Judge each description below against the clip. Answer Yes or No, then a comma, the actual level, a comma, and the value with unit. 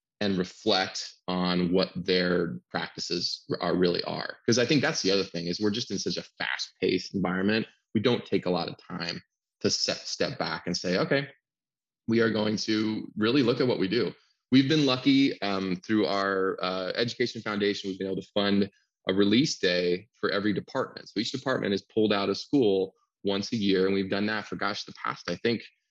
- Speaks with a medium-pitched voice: No, low, 100 Hz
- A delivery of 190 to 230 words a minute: Yes, fast, 205 wpm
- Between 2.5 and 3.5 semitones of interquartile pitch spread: Yes, average, 2.9 semitones